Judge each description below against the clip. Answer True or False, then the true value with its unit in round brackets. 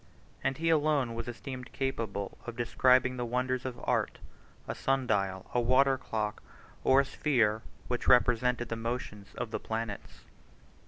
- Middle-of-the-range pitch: False (125 Hz)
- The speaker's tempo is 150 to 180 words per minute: True (155 wpm)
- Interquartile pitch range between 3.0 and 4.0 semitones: False (2.4 semitones)